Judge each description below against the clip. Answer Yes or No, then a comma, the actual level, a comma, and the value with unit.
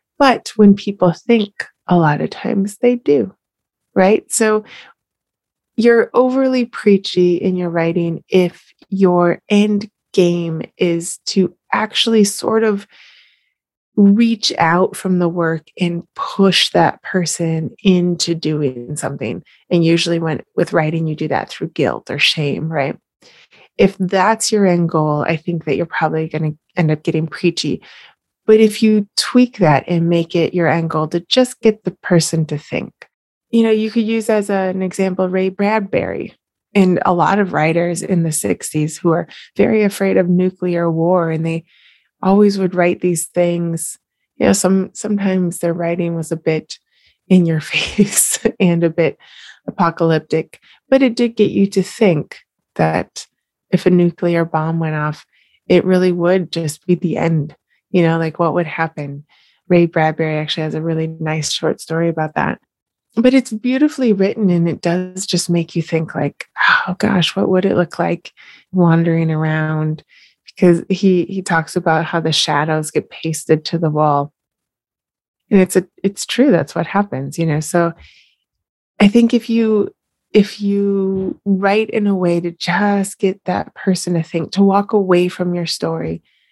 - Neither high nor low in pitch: Yes, medium, 175 Hz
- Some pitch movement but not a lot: Yes, average, 3.5 semitones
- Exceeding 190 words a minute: No, average, 165 wpm